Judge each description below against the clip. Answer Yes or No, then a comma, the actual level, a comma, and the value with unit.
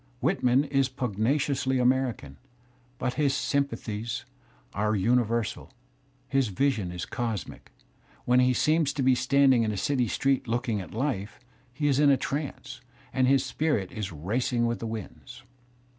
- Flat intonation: No, average, 3.7 semitones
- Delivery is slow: No, average, 155 wpm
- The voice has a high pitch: No, low, 125 Hz